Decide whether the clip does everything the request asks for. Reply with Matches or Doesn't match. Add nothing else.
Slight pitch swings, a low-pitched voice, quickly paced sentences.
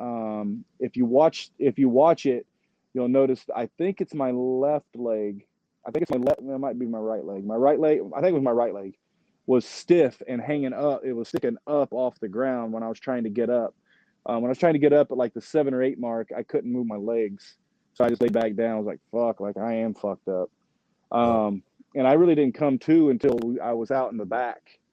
Doesn't match